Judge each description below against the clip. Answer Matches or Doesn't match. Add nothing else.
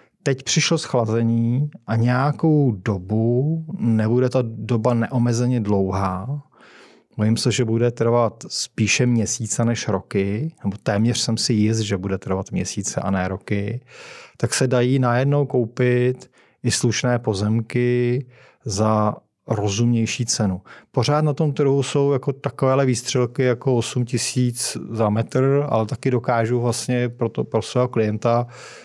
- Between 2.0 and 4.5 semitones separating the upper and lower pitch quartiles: Matches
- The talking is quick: Doesn't match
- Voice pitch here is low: Matches